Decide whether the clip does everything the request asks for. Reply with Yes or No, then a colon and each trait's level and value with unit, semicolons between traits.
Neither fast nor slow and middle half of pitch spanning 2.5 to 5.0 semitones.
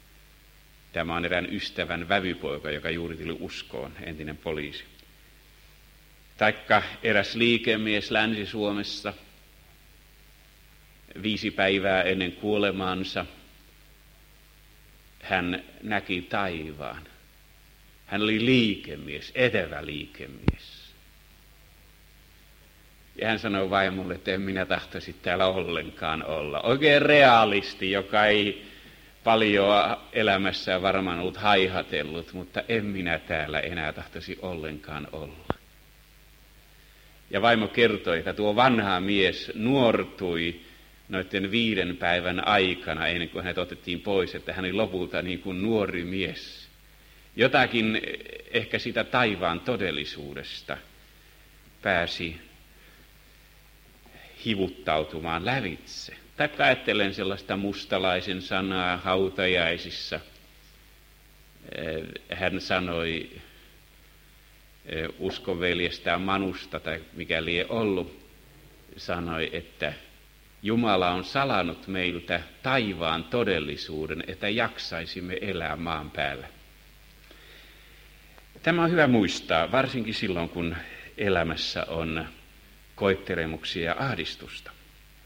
No: slow, 90 wpm; average, 4.0 semitones